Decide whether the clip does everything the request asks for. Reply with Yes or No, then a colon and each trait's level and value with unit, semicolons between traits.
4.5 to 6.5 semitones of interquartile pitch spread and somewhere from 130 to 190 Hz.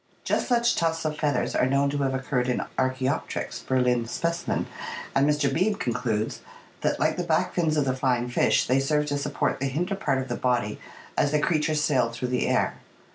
No: average, 3.2 semitones; low, 135 Hz